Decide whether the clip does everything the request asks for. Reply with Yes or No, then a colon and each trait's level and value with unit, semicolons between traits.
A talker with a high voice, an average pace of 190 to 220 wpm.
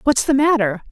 Yes: very high, 255 Hz; average, 200 wpm